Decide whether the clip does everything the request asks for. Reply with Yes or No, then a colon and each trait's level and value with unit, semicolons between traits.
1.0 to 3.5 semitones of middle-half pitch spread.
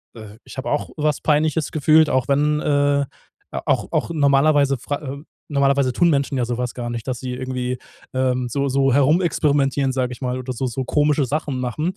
Yes: narrow, 2.5 semitones